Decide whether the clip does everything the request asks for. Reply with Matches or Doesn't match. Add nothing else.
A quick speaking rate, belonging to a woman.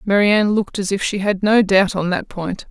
Matches